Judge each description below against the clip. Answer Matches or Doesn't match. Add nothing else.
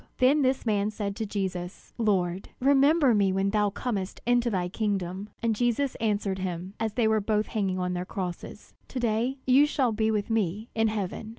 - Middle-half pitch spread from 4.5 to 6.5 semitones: Doesn't match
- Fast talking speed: Doesn't match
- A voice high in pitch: Matches